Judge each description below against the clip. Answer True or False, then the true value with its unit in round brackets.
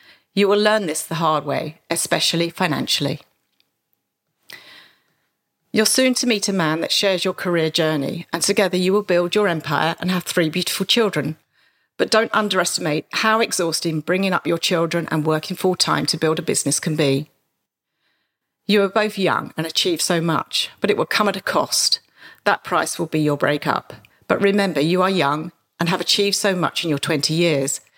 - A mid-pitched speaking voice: True (170 Hz)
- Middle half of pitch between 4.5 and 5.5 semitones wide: False (4.0 semitones)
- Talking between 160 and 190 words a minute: True (185 wpm)